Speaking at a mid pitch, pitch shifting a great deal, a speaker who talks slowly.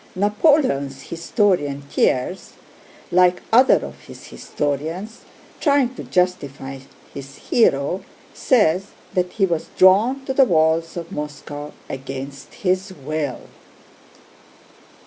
Yes: medium, 170 Hz; wide, 6.2 semitones; slow, 105 wpm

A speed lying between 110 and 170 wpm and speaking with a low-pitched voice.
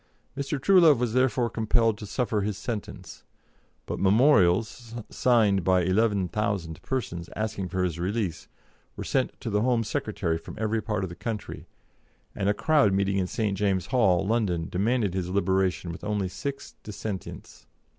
Yes: average, 155 wpm; low, 105 Hz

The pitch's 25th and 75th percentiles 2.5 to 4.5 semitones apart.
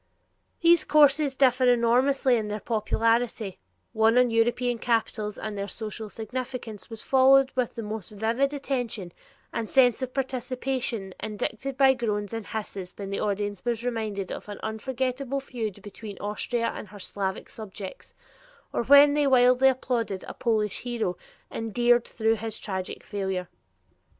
Yes: average, 3.5 semitones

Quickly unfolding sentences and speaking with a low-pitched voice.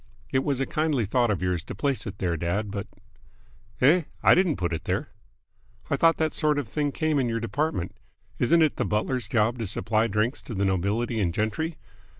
Yes: fast, 210 wpm; low, 115 Hz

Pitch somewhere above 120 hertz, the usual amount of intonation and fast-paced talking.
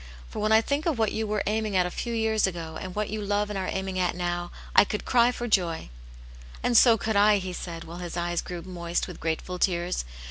Yes: high, 190 Hz; average, 3.7 semitones; fast, 245 wpm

